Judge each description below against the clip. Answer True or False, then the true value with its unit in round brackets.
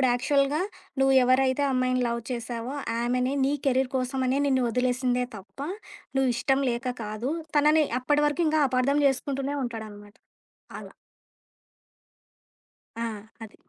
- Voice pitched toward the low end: False (255 Hz)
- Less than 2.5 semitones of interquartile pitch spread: True (2.0 semitones)